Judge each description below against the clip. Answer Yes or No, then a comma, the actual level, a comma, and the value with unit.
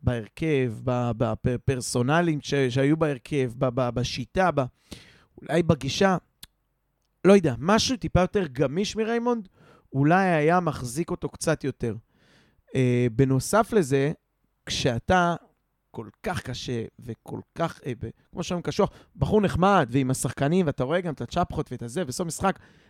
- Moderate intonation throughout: No, wide, 5.7 semitones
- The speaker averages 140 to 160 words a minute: No, average, 120 wpm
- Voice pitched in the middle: Yes, medium, 145 Hz